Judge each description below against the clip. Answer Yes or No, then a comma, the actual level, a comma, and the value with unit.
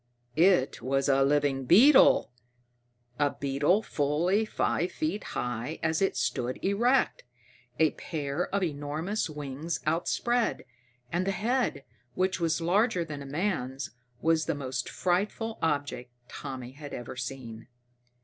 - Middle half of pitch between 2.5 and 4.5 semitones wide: No, wide, 5.5 semitones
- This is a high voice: No, medium, 155 Hz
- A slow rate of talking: Yes, slow, 130 wpm